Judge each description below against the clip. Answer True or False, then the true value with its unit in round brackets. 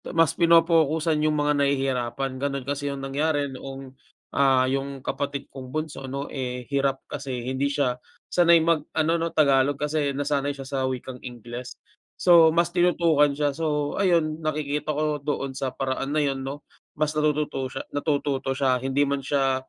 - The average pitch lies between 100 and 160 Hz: True (140 Hz)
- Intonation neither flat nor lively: False (2.3 semitones)